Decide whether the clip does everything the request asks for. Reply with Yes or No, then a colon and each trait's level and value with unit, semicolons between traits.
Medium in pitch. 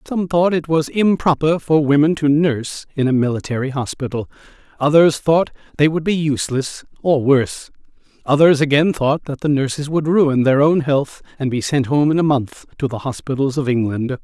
Yes: medium, 145 Hz